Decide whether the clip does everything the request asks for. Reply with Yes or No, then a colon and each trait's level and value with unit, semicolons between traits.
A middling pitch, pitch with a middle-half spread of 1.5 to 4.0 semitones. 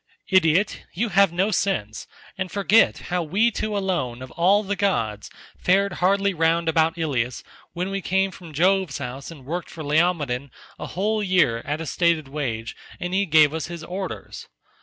No: medium, 175 Hz; average, 4.4 semitones